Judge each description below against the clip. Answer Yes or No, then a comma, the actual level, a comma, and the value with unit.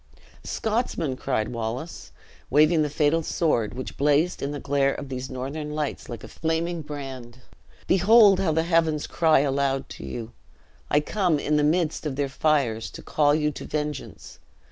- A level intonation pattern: No, average, 3.2 semitones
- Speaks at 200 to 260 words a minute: No, average, 165 wpm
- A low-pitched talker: No, medium, 150 Hz